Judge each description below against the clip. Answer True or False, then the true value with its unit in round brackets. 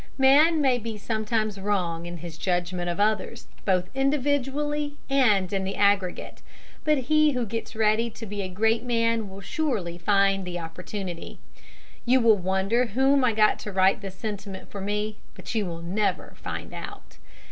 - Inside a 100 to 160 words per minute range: False (170 wpm)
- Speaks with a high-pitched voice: True (210 Hz)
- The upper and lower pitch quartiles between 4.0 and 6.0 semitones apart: True (4.3 semitones)